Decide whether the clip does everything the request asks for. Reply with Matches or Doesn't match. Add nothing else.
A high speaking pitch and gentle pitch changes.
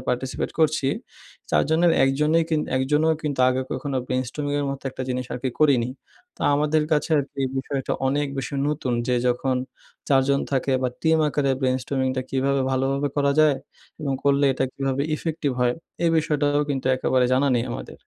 Doesn't match